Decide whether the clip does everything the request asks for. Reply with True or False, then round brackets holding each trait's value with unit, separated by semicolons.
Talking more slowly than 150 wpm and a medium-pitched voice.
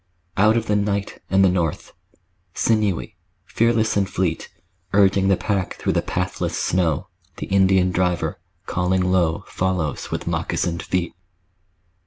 False (135 wpm; 95 Hz)